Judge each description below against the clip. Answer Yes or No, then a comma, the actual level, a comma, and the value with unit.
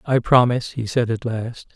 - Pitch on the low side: Yes, low, 120 Hz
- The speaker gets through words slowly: No, fast, 205 wpm